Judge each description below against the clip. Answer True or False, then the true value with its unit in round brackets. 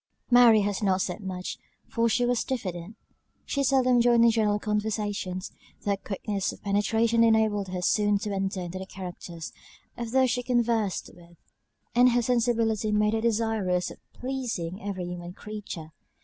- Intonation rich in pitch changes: False (3.5 semitones)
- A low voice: False (210 Hz)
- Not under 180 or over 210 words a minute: False (165 wpm)